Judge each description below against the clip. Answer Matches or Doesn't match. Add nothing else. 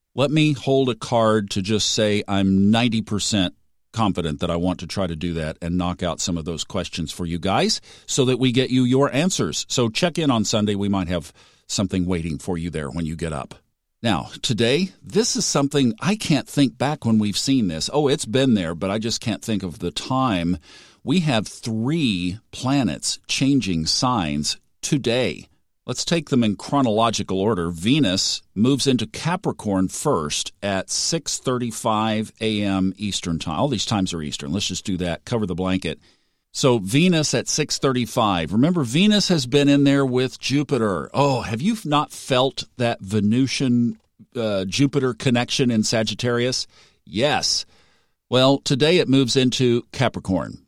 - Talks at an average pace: Matches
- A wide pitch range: Matches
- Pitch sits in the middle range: Doesn't match